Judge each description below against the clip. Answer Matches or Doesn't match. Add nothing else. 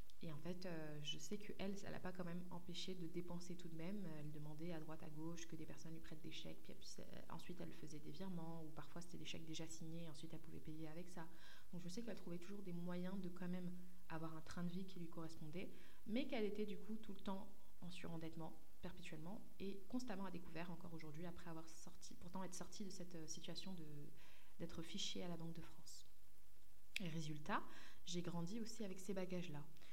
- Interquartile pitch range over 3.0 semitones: Doesn't match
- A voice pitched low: Doesn't match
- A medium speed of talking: Doesn't match